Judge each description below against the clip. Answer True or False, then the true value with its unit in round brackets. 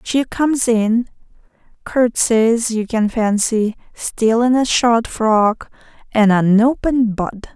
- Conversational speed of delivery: False (110 wpm)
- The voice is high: True (230 Hz)